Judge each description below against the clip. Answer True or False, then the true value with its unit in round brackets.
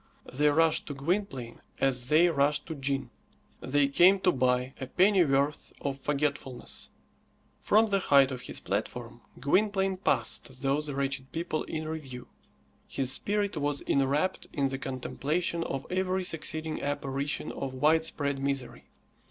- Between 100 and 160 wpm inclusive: True (135 wpm)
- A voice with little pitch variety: False (3.3 semitones)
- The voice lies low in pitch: False (145 Hz)